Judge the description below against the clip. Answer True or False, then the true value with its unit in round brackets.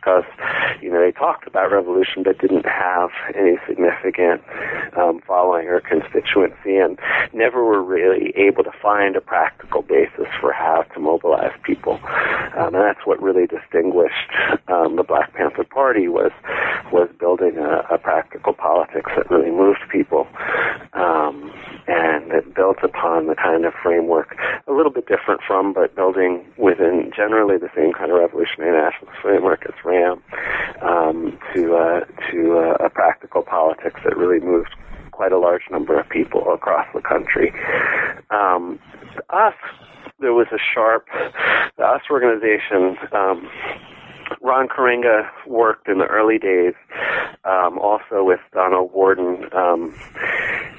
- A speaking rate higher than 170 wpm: False (145 wpm)